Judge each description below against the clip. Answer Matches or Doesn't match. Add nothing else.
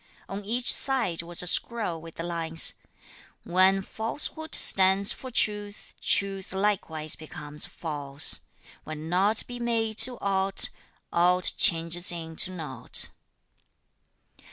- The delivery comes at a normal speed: Doesn't match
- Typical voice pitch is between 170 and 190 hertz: Matches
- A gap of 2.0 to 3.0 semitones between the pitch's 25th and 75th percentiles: Doesn't match